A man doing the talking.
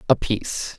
No: female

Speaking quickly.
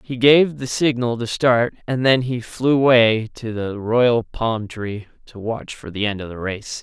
Yes: fast, 210 wpm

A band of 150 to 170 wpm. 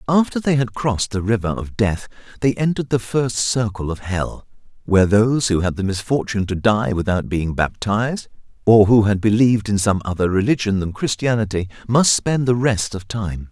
No: average, 185 wpm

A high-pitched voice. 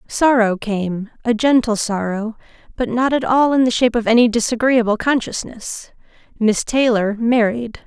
Yes: high, 230 Hz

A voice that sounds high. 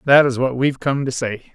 No: low, 130 Hz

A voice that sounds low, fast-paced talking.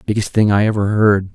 Yes: low, 105 Hz; fast, 220 wpm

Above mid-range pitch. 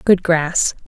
No: medium, 170 Hz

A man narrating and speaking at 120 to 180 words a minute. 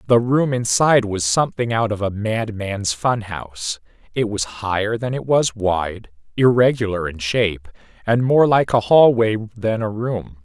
Yes: male; average, 160 wpm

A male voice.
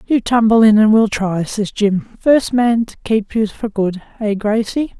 No: female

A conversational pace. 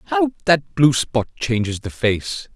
Yes: average, 165 wpm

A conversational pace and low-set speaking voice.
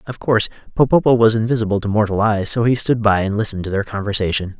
No: fast, 220 wpm; low, 110 Hz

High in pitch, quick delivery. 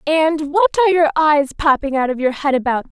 Yes: very high, 295 Hz; fast, 220 wpm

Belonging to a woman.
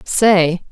Yes: female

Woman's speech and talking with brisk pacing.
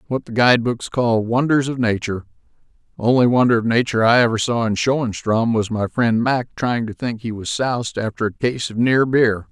No: male; fast, 210 wpm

